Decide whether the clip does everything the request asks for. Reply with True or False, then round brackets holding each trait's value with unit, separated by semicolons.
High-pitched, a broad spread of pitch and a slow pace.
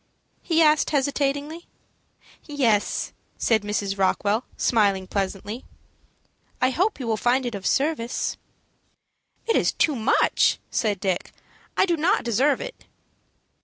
True (245 Hz; 6.1 semitones; 125 wpm)